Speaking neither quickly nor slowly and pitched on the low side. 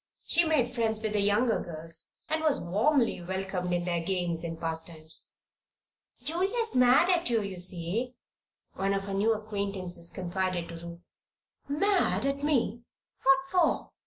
No: average, 150 wpm; high, 200 Hz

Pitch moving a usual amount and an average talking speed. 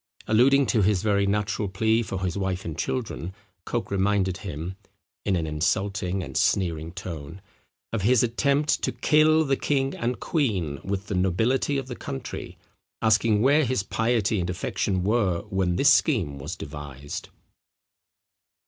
Yes: average, 4.8 semitones; average, 150 wpm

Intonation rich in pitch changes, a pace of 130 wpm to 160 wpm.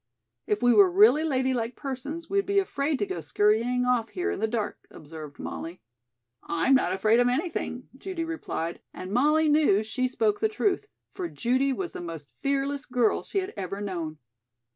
No: wide, 7.2 semitones; average, 180 wpm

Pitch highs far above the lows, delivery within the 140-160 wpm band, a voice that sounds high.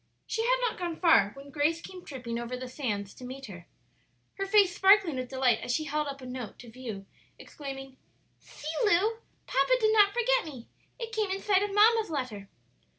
No: wide, 8.1 semitones; average, 195 wpm; very high, 300 Hz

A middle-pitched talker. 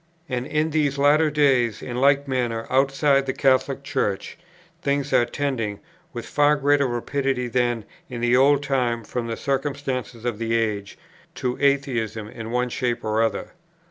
No: low, 130 Hz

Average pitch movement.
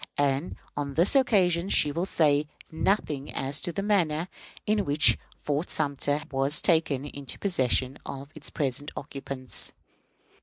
Yes: average, 3.6 semitones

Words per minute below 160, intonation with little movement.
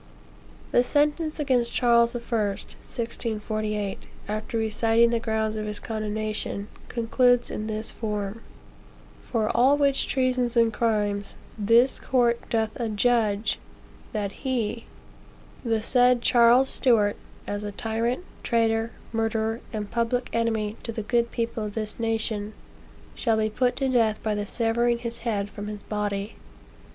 Yes: average, 140 wpm; narrow, 2.0 semitones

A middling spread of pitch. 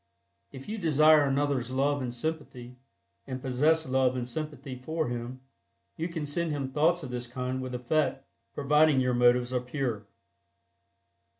Yes: average, 3.4 semitones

